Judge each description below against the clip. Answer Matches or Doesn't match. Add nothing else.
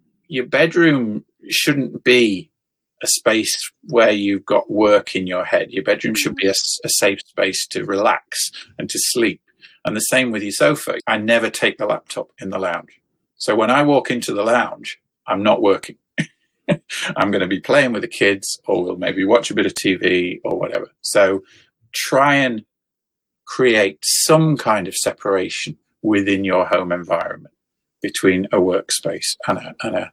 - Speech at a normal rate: Matches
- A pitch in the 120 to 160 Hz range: Doesn't match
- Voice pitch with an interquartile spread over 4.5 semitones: Matches